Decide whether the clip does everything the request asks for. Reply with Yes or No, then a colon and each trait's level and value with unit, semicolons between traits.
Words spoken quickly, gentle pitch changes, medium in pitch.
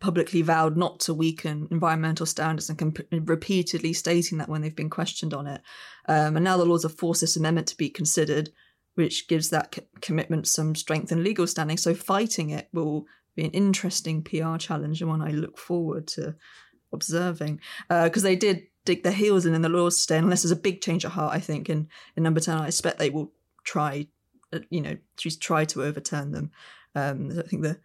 Yes: fast, 210 wpm; narrow, 1.8 semitones; medium, 165 Hz